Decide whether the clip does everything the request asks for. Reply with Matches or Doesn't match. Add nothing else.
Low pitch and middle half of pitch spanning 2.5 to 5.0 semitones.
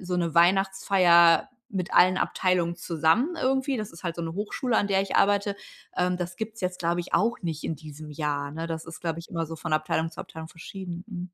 Doesn't match